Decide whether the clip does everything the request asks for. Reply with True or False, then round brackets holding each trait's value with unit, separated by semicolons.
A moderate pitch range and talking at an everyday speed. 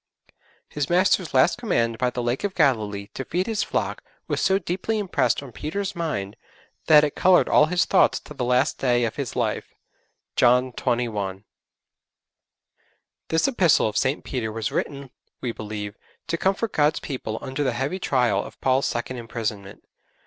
False (6.2 semitones; 165 wpm)